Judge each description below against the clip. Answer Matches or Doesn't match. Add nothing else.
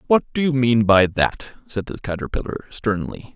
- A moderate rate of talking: Matches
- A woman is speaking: Doesn't match